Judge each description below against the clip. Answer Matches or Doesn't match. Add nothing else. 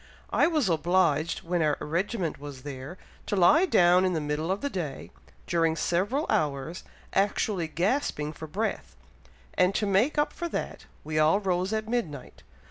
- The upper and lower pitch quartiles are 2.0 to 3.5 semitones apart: Doesn't match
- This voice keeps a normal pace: Matches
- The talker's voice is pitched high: Doesn't match